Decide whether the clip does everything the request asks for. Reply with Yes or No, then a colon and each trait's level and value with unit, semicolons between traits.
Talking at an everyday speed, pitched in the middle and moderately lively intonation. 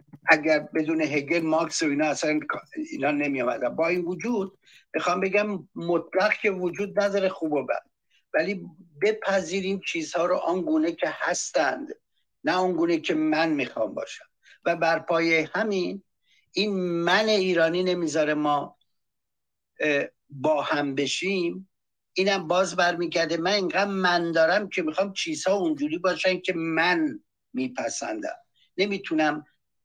Yes: average, 130 wpm; medium, 180 Hz; average, 3.5 semitones